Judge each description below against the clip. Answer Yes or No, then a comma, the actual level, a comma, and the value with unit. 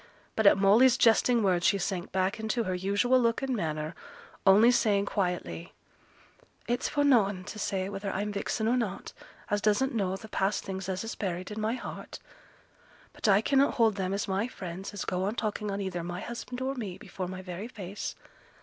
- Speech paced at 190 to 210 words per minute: Yes, average, 195 wpm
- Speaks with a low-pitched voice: No, high, 200 Hz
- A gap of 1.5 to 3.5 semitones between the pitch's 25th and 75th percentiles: Yes, average, 3.2 semitones